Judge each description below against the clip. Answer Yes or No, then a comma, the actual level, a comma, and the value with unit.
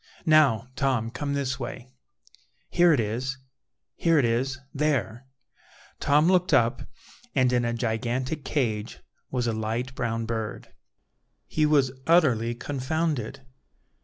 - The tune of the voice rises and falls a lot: No, average, 3.8 semitones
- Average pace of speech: No, slow, 125 wpm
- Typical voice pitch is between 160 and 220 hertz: No, low, 130 Hz